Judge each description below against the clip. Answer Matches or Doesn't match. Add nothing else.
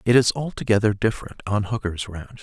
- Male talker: Matches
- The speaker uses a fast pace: Doesn't match